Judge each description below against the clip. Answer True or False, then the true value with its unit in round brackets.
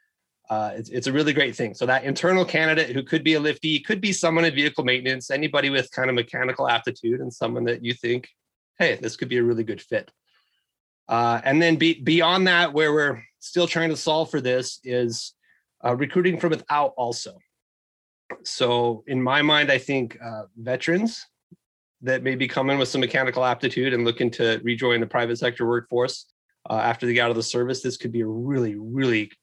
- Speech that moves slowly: False (200 wpm)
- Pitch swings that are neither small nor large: True (4.2 semitones)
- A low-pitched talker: True (130 Hz)